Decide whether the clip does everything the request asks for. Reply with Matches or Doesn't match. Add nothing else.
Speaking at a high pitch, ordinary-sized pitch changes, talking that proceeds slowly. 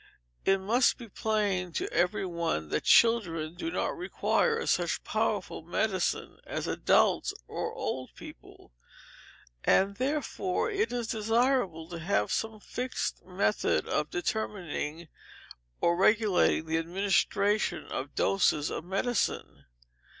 Matches